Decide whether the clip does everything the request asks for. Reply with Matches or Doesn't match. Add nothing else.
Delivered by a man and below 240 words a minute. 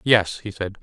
Matches